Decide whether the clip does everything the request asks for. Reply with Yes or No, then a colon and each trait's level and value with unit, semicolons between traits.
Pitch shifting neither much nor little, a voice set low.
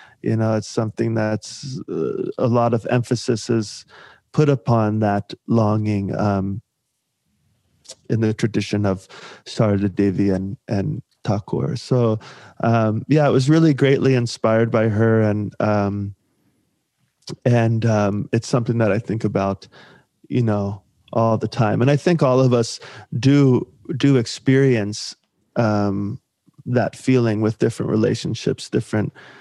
Yes: average, 3.6 semitones; low, 115 Hz